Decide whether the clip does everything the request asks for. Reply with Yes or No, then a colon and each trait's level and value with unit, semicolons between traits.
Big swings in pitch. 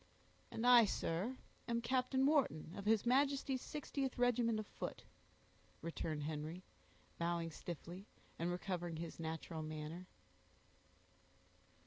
Yes: wide, 6.9 semitones